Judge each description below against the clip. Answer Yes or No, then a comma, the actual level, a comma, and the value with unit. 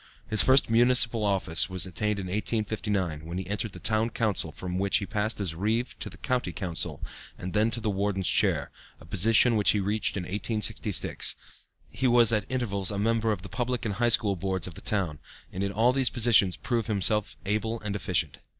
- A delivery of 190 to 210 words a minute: Yes, fast, 205 wpm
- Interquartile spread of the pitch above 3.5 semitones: No, average, 3.2 semitones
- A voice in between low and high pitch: No, low, 105 Hz